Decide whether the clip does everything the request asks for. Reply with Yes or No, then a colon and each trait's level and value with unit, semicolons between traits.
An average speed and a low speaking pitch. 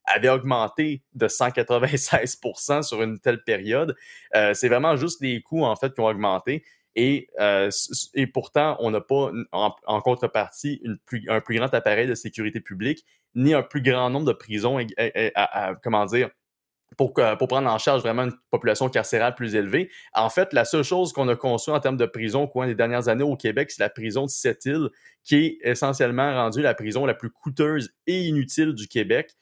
Yes: average, 205 wpm; low, 125 Hz